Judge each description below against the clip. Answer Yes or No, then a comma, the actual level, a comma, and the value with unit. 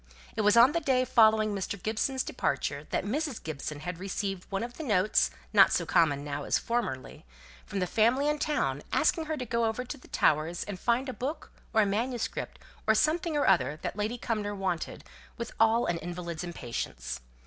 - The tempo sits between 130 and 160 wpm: No, average, 190 wpm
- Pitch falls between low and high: No, high, 215 Hz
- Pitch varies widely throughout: Yes, wide, 6.1 semitones